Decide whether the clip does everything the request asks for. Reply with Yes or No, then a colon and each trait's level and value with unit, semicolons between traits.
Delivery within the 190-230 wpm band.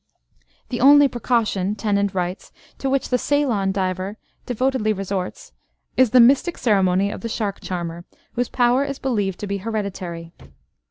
No: average, 150 wpm